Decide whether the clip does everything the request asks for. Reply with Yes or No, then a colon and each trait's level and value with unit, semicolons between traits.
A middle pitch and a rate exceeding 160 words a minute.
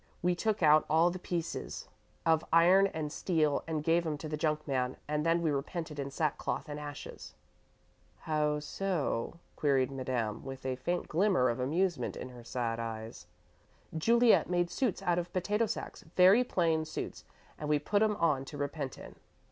Yes: medium, 155 Hz; average, 175 wpm